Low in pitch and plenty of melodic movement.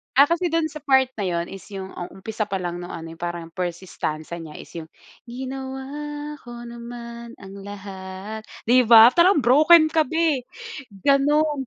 No: high, 235 Hz; wide, 7.4 semitones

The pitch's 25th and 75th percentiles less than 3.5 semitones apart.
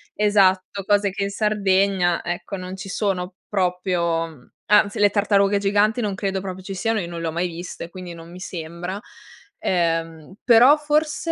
Yes: narrow, 2.6 semitones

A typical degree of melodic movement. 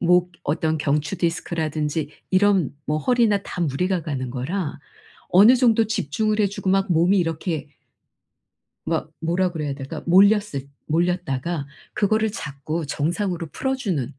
Yes: average, 4.8 semitones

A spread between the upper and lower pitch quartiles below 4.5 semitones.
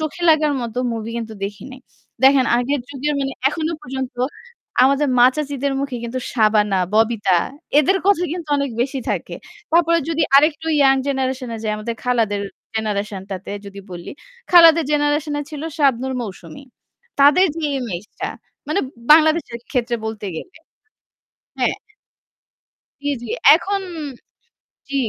No: average, 5.2 semitones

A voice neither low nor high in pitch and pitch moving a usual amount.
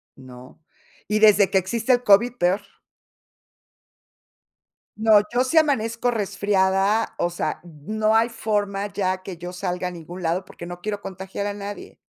No: high, 200 Hz; average, 3.3 semitones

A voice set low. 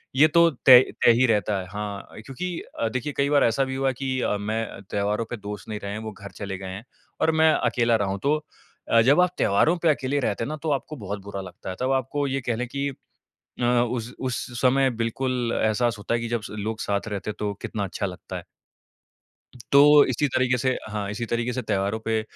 Yes: low, 115 Hz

